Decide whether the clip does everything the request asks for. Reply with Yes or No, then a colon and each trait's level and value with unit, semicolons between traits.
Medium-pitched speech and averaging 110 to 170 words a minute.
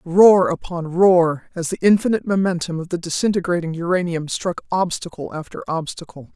Yes: medium, 175 Hz; average, 140 wpm